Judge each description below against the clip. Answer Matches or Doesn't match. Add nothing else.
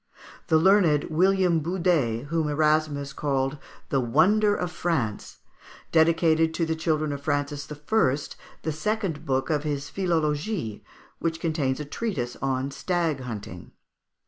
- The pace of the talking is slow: Matches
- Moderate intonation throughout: Matches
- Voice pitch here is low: Doesn't match